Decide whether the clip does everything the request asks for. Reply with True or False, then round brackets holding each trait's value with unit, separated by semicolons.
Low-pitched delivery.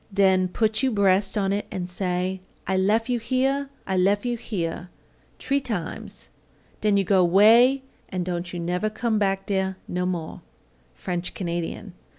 False (195 Hz)